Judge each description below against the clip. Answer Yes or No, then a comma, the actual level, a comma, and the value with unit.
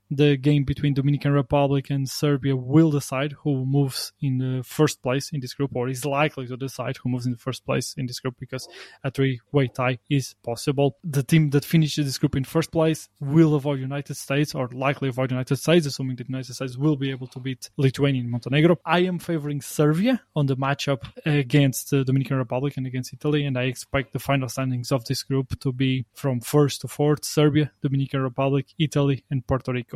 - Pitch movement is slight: Yes, narrow, 2.0 semitones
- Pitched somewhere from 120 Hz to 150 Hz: Yes, medium, 140 Hz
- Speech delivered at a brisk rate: Yes, fast, 210 wpm